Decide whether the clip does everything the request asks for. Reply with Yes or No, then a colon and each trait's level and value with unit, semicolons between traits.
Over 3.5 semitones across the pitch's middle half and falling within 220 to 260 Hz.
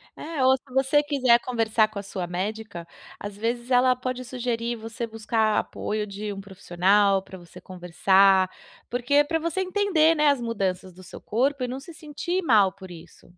Yes: average, 5.2 semitones; high, 230 Hz